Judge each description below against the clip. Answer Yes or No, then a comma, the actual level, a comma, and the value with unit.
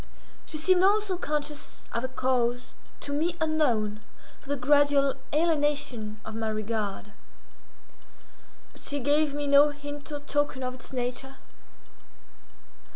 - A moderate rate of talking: No, slow, 130 wpm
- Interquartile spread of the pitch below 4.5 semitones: Yes, average, 3.2 semitones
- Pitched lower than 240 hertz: No, very high, 285 Hz